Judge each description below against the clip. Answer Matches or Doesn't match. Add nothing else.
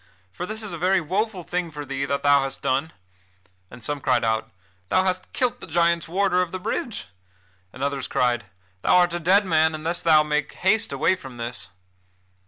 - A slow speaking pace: Doesn't match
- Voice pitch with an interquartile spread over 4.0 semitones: Matches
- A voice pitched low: Doesn't match